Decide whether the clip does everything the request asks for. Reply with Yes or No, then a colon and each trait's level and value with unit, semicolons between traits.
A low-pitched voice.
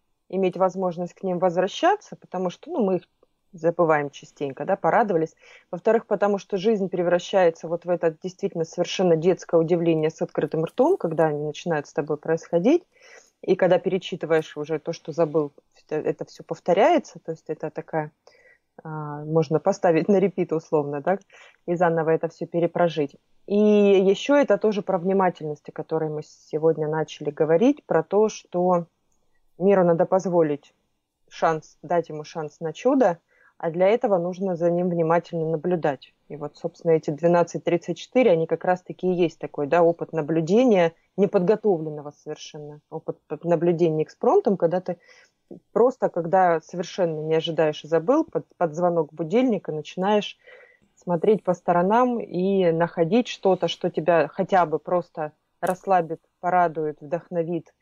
No: medium, 170 Hz